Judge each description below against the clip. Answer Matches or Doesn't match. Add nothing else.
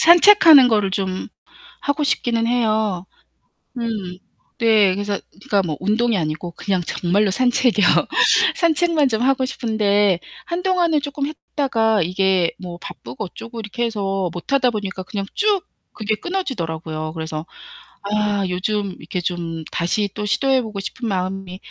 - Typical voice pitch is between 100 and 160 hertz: Doesn't match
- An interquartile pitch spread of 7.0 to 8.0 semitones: Doesn't match